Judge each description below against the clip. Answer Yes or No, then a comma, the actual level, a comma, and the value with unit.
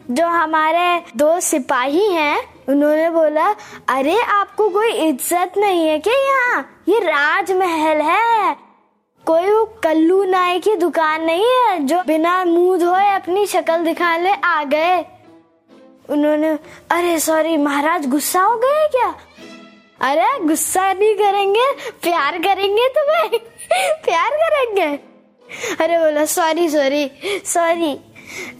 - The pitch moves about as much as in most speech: Yes, average, 4.0 semitones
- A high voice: Yes, very high, 340 Hz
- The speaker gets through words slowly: No, average, 120 wpm